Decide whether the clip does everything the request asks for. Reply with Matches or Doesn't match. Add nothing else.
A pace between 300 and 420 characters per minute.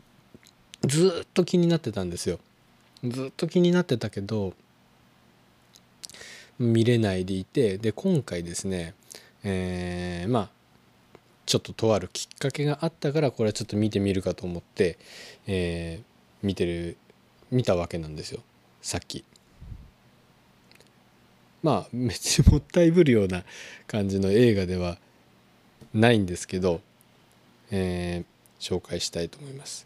Doesn't match